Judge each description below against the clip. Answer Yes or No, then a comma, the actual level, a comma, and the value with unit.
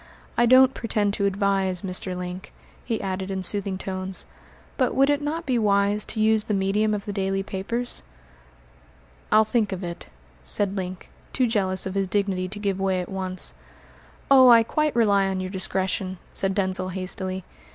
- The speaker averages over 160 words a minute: Yes, average, 175 wpm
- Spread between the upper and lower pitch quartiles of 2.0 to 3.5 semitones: Yes, narrow, 2.4 semitones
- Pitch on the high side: Yes, high, 195 Hz